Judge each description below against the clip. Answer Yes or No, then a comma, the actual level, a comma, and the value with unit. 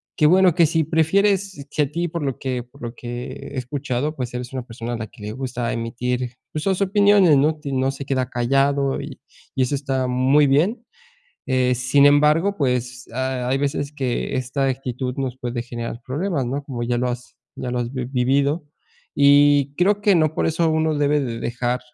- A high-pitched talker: No, low, 135 Hz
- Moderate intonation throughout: Yes, average, 3.2 semitones